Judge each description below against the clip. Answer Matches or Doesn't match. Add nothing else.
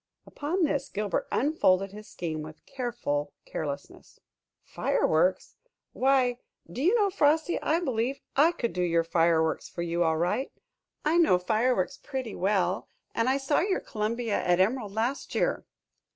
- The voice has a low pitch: Doesn't match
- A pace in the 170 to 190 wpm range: Doesn't match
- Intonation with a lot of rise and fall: Matches